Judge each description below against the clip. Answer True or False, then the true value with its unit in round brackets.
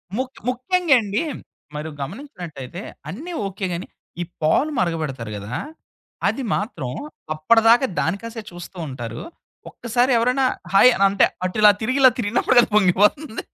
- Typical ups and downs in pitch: False (7.3 semitones)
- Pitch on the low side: False (205 Hz)